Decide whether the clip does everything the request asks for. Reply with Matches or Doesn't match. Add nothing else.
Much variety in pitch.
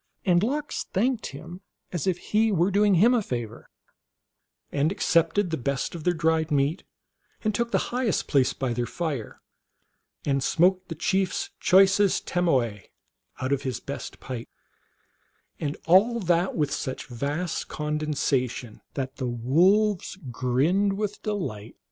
Matches